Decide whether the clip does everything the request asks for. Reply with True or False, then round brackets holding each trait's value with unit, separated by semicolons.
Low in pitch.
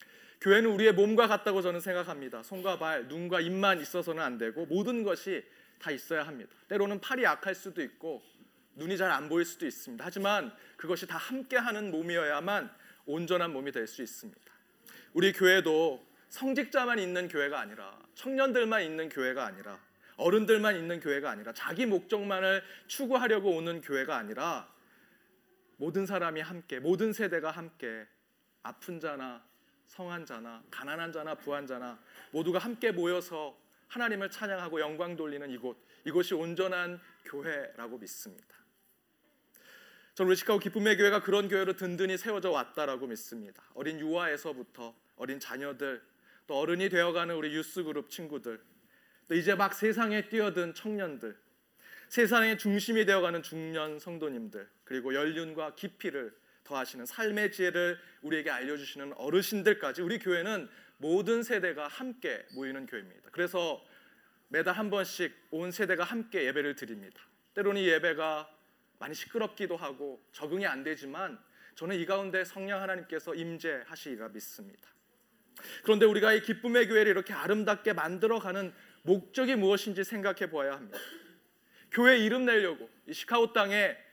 False (185 Hz)